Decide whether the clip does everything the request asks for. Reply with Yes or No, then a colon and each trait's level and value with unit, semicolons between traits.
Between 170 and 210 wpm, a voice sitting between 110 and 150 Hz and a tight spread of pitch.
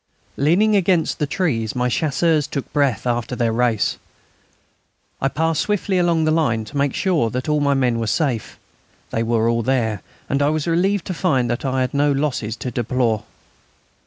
No: average, 185 wpm; medium, 140 Hz; average, 5.2 semitones